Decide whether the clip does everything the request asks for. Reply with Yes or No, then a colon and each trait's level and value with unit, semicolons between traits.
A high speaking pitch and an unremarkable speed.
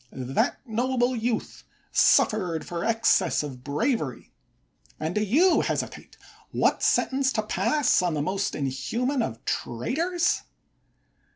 No: high, 215 Hz; slow, 115 wpm